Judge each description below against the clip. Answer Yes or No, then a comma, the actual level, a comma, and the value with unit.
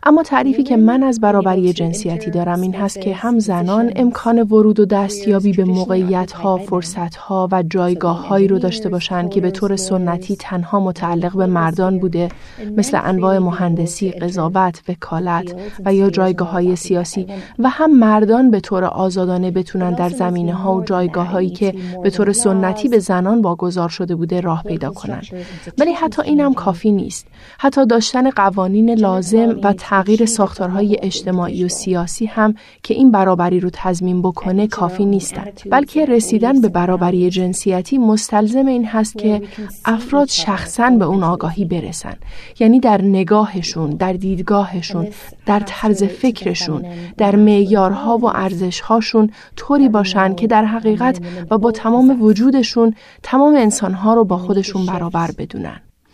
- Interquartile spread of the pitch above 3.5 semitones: No, average, 3.2 semitones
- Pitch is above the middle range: Yes, high, 195 Hz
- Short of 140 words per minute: No, average, 150 wpm